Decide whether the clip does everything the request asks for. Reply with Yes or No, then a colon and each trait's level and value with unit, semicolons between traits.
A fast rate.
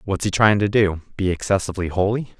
No: average, 175 wpm